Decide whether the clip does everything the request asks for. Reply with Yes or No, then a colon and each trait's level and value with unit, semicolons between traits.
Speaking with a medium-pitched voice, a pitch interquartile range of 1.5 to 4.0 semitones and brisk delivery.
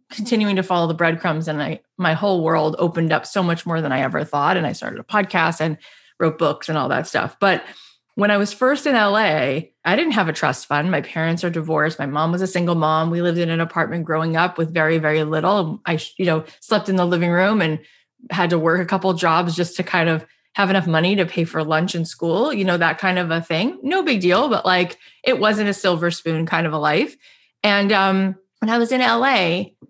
Yes: medium, 175 Hz; average, 3.2 semitones; fast, 245 wpm